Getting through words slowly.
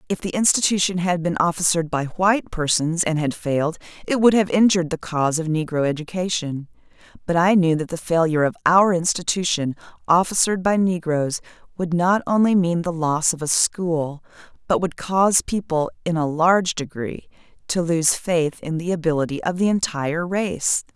No: average, 170 wpm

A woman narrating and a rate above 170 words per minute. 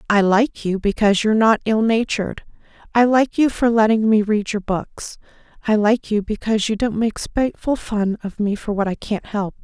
Yes: female; average, 200 wpm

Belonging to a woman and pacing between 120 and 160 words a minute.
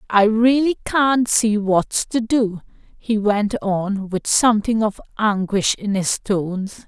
Yes: female; average, 150 wpm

